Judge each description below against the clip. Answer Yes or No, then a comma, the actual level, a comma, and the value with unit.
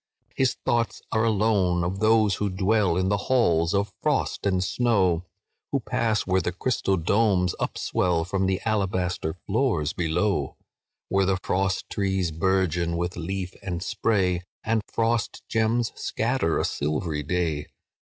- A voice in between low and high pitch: No, very low, 95 Hz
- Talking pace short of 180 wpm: Yes, average, 140 wpm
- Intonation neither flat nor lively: Yes, average, 3.7 semitones